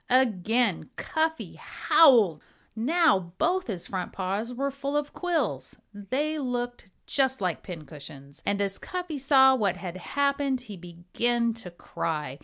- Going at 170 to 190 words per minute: No, slow, 135 wpm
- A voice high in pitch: Yes, high, 235 Hz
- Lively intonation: Yes, wide, 7.4 semitones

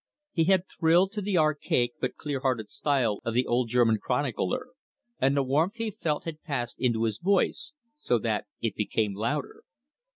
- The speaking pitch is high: No, low, 135 Hz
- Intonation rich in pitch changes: Yes, wide, 6.0 semitones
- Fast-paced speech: No, average, 175 wpm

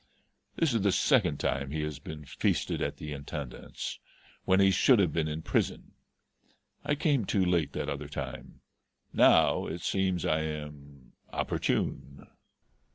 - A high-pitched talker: No, very low, 80 Hz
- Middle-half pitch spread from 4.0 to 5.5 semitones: Yes, average, 4.9 semitones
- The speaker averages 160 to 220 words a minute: No, average, 150 wpm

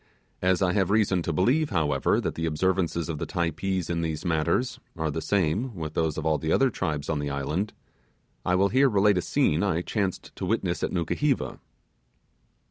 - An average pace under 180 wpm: No, average, 190 wpm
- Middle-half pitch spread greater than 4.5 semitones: No, average, 3.8 semitones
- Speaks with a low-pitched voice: Yes, very low, 85 Hz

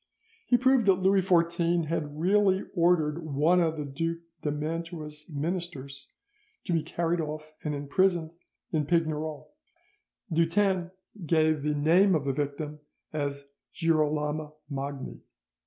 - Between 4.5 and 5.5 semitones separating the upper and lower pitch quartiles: No, narrow, 2.5 semitones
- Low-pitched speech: No, medium, 160 Hz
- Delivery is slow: Yes, slow, 125 wpm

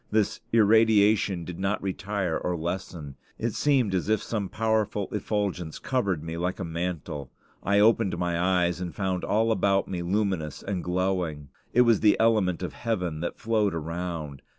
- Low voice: Yes, very low, 95 Hz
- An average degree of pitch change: Yes, average, 3.6 semitones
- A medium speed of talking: Yes, average, 165 wpm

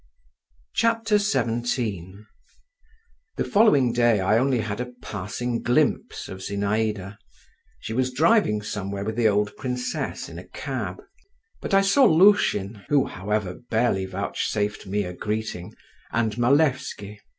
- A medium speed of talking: No, slow, 125 wpm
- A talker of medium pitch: No, low, 110 Hz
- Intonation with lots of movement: No, average, 4.0 semitones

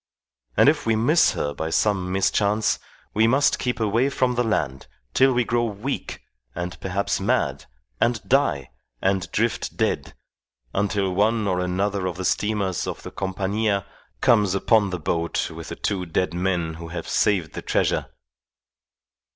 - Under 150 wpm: No, average, 160 wpm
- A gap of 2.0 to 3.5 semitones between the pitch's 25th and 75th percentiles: No, average, 3.9 semitones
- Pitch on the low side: Yes, low, 100 Hz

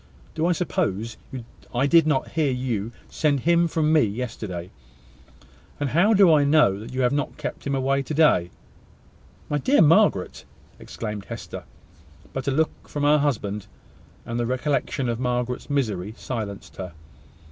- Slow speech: No, average, 160 wpm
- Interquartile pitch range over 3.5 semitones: Yes, average, 5.1 semitones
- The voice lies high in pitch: No, low, 135 Hz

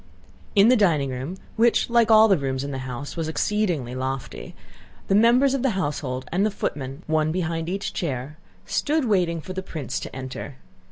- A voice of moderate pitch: Yes, medium, 165 Hz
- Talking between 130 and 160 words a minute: No, average, 175 wpm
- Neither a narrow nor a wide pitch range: No, wide, 7.4 semitones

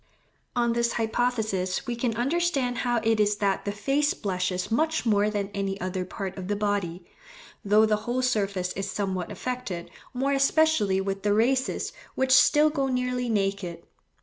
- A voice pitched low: No, high, 215 Hz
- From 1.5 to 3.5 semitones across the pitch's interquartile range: No, average, 4.3 semitones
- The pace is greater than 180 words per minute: No, average, 165 wpm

